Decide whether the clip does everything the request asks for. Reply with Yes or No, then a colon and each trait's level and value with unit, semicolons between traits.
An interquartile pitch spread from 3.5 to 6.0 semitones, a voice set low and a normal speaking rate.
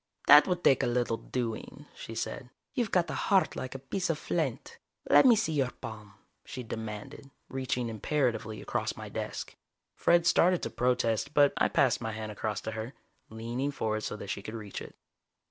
Yes: average, 5.0 semitones; low, 125 Hz; average, 190 wpm